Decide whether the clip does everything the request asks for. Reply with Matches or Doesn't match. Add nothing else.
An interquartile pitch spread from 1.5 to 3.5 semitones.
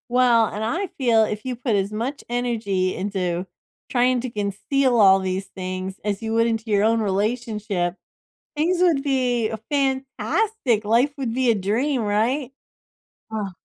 Doesn't match